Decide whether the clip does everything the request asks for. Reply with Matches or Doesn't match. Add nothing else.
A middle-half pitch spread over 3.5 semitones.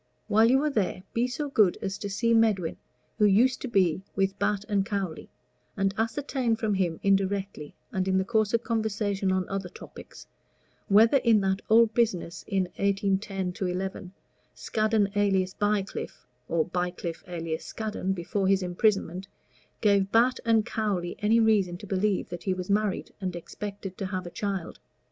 Doesn't match